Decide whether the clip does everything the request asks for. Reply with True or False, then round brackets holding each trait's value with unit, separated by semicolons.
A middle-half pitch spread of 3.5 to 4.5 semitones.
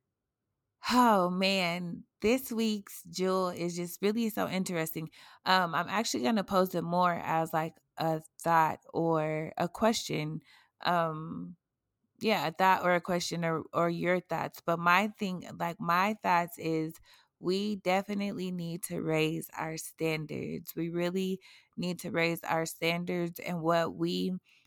False (2.5 semitones)